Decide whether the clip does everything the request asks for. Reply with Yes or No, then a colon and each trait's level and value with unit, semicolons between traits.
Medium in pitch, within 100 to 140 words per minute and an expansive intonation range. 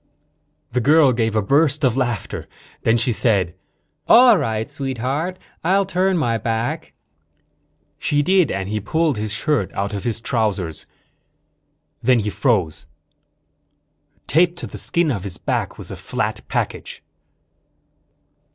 No: low, 120 Hz; slow, 135 wpm; wide, 6.3 semitones